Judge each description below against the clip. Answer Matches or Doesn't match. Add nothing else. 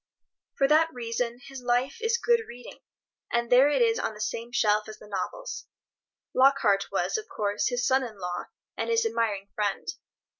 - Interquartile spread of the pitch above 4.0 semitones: Matches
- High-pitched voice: Matches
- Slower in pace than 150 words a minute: Doesn't match